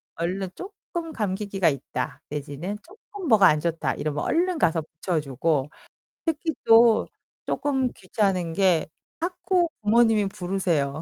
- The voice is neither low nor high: No, high, 195 Hz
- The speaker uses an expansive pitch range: Yes, wide, 7.9 semitones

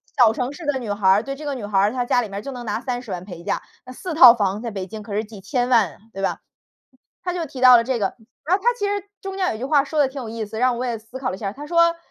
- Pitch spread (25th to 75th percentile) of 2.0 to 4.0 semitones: No, average, 4.9 semitones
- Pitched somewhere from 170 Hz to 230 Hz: No, high, 245 Hz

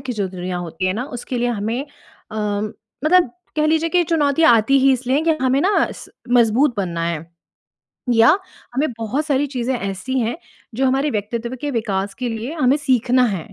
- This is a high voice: Yes, high, 245 Hz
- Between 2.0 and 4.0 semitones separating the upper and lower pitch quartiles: No, average, 4.8 semitones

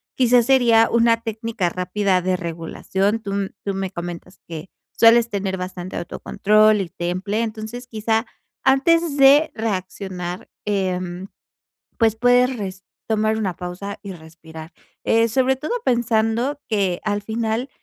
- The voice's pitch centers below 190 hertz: No, high, 210 Hz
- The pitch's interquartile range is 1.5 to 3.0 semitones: No, average, 3.9 semitones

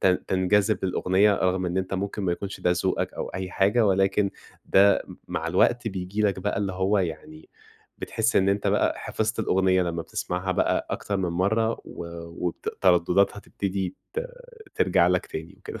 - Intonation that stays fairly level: Yes, narrow, 1.9 semitones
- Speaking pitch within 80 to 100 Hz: Yes, very low, 95 Hz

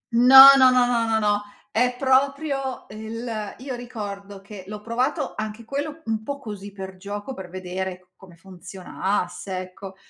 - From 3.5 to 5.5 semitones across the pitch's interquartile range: Yes, average, 4.7 semitones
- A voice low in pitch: No, high, 215 Hz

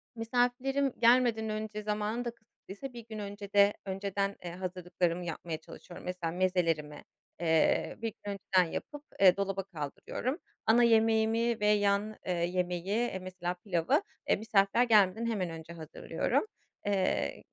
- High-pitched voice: Yes, high, 200 Hz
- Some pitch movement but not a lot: Yes, average, 3.9 semitones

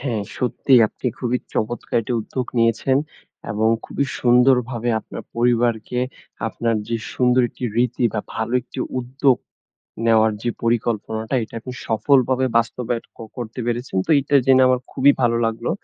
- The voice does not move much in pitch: Yes, narrow, 1.9 semitones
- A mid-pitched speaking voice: No, low, 120 Hz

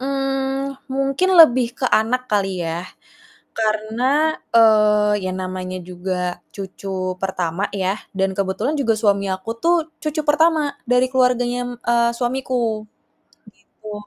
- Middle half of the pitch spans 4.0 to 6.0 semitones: Yes, average, 5.2 semitones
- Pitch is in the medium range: No, high, 230 Hz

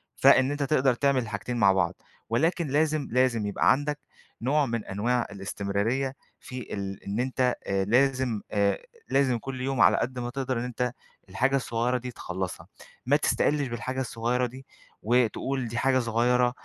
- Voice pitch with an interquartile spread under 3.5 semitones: Yes, average, 2.8 semitones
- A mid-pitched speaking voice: No, low, 125 Hz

